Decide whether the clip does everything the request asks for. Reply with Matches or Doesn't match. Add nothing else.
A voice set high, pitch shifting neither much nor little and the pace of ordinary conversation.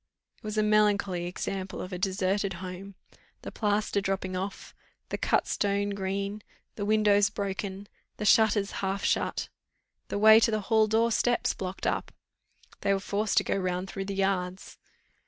Doesn't match